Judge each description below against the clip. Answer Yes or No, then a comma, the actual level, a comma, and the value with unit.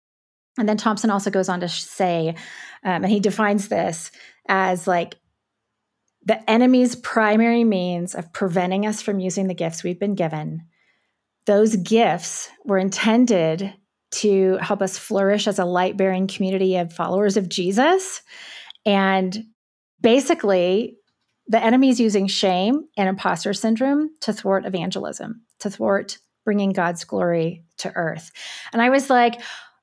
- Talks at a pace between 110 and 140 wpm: Yes, slow, 135 wpm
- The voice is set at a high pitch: Yes, high, 200 Hz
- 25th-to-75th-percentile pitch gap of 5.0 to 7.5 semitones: No, average, 3.3 semitones